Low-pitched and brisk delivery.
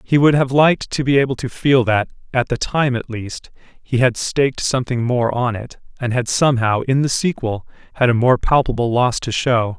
Yes: low, 125 Hz; fast, 215 wpm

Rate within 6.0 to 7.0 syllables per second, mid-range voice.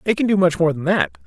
Yes: 6.1 syllables/s; medium, 160 Hz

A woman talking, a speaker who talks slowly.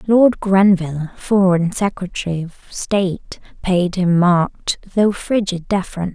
Yes: female; slow, 100 wpm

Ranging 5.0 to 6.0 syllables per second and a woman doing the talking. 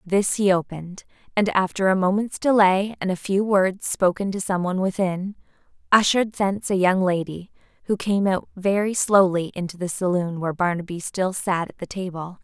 Yes: 5.2 syllables/s; female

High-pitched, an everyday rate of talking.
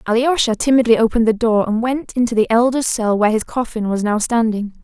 No: high, 230 Hz; fast, 210 wpm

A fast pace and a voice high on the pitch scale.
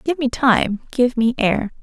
No: average, 195 wpm; high, 240 Hz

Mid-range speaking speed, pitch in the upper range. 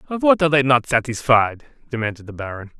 No: average, 195 wpm; low, 130 Hz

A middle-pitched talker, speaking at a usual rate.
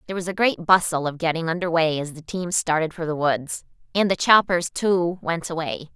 No: medium, 170 Hz; fast, 220 wpm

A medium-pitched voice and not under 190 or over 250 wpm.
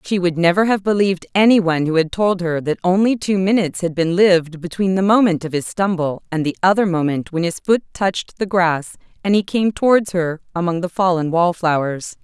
Yes: medium, 180 Hz; fast, 205 wpm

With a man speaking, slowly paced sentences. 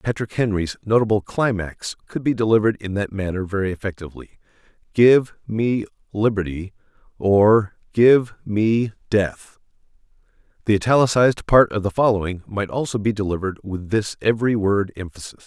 Yes: male; slow, 110 wpm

